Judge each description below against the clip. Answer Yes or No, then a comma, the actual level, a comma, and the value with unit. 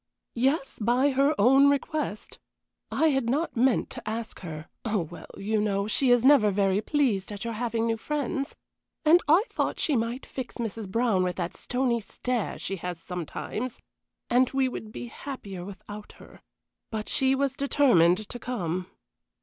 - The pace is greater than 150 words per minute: Yes, average, 165 wpm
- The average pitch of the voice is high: Yes, high, 230 Hz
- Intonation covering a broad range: No, average, 4.9 semitones